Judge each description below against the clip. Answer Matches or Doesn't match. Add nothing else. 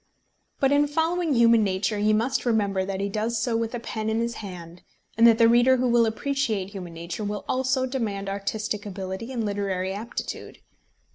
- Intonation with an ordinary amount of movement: Matches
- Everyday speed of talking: Matches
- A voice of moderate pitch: Doesn't match